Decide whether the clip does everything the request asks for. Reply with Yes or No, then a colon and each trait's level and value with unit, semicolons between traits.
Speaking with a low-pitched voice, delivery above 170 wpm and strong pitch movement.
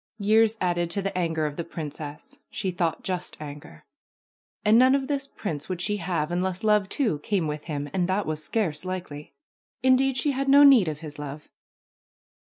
No: medium, 180 Hz; average, 185 wpm; wide, 6.1 semitones